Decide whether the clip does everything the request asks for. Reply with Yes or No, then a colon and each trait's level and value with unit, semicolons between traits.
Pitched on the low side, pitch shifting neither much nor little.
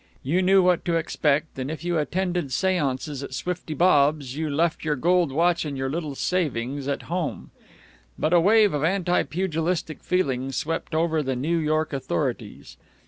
No: medium, 160 Hz; average, 3.9 semitones